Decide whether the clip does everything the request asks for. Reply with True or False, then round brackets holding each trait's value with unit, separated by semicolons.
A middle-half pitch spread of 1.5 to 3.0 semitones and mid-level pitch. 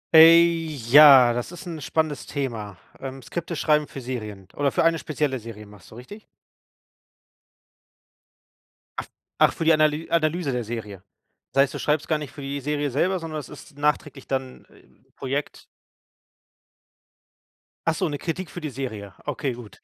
False (4.3 semitones; 145 Hz)